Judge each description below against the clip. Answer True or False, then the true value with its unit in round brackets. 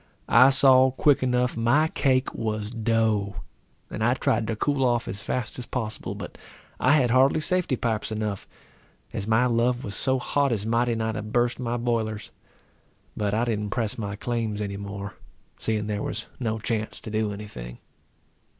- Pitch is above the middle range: False (115 Hz)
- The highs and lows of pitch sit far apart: False (2.8 semitones)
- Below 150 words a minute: False (180 wpm)